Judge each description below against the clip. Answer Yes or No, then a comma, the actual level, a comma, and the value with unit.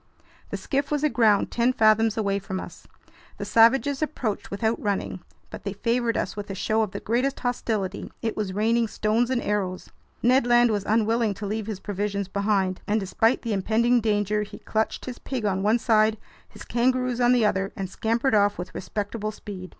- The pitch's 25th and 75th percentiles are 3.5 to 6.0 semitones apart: No, average, 2.8 semitones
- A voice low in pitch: No, high, 220 Hz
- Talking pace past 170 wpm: Yes, average, 190 wpm